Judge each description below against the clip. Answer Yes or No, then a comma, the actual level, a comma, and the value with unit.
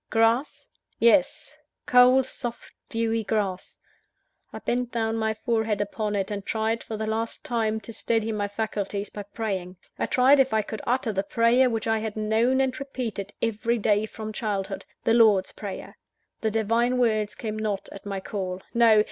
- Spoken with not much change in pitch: Yes, narrow, 2.1 semitones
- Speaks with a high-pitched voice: Yes, high, 220 Hz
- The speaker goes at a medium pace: Yes, average, 170 wpm